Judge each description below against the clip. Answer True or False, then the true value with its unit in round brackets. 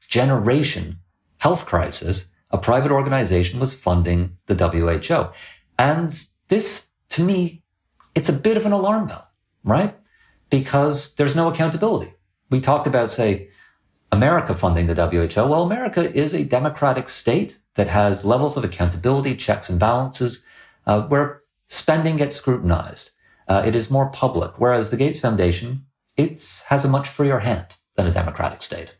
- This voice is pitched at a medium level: False (125 Hz)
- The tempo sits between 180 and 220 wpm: False (150 wpm)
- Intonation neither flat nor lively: False (7.5 semitones)